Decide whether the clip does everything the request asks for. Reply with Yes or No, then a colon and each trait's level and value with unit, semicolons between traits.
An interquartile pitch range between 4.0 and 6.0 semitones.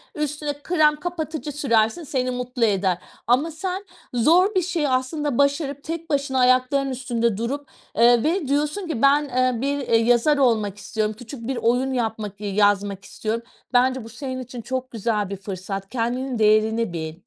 Yes: average, 4.5 semitones